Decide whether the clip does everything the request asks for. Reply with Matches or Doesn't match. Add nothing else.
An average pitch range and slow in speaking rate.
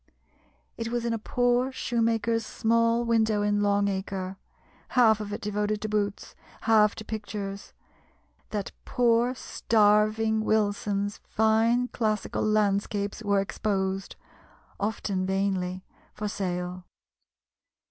Doesn't match